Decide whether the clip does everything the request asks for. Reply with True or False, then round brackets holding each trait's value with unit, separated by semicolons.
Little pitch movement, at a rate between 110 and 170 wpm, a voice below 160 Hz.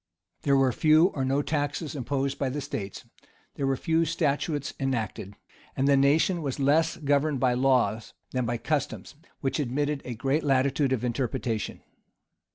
True (2.3 semitones; 160 wpm; 140 Hz)